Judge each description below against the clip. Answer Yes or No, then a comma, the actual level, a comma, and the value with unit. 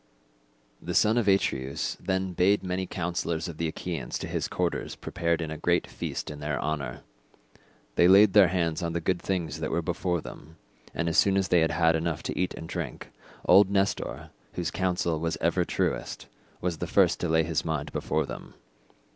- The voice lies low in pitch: Yes, very low, 85 Hz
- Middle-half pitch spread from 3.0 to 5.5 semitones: No, narrow, 2.5 semitones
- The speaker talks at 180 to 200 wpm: Yes, average, 190 wpm